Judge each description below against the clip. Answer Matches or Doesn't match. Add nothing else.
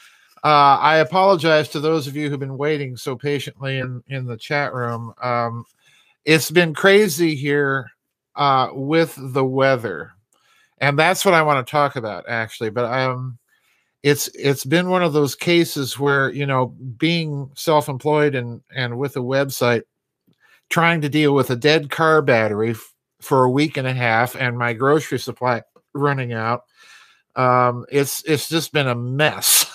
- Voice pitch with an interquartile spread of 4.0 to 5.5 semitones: Doesn't match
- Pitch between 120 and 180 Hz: Matches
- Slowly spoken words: Doesn't match